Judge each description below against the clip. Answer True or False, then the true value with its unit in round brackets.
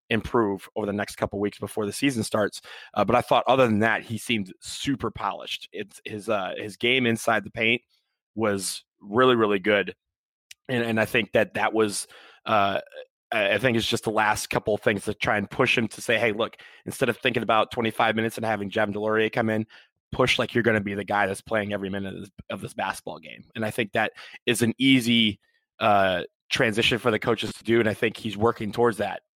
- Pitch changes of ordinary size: False (2.1 semitones)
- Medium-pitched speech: False (110 Hz)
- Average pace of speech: False (225 wpm)